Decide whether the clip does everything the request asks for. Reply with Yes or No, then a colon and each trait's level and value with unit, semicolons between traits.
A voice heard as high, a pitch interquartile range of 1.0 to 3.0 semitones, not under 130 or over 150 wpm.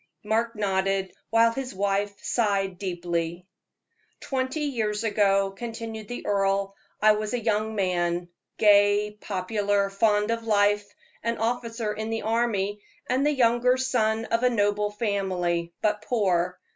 Yes: high, 210 Hz; narrow, 2.6 semitones; slow, 135 wpm